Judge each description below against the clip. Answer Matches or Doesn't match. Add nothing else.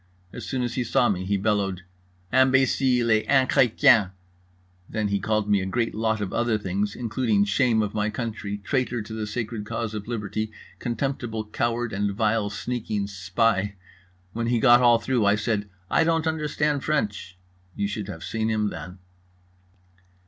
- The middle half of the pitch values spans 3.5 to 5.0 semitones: Doesn't match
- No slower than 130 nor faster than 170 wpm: Matches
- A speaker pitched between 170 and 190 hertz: Doesn't match